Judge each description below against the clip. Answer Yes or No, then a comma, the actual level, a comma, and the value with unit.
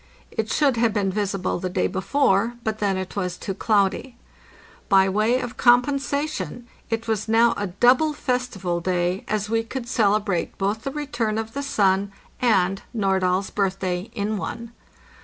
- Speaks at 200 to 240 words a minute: No, average, 160 wpm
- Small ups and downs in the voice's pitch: No, average, 3.8 semitones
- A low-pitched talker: No, high, 215 Hz